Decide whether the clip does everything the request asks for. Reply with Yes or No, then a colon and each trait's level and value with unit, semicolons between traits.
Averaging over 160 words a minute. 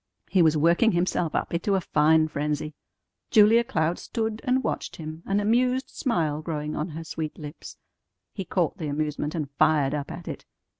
Yes: average, 180 wpm